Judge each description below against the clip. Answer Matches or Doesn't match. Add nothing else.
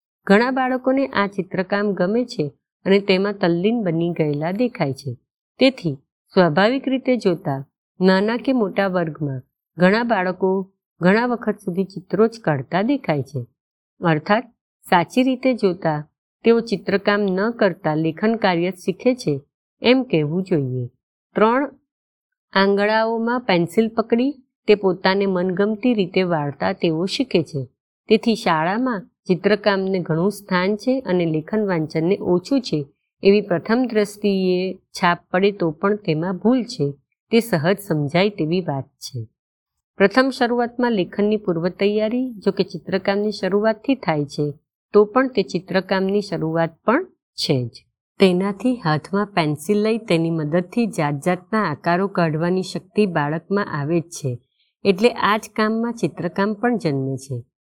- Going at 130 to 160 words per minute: Matches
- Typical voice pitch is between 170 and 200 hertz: Matches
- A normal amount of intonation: Matches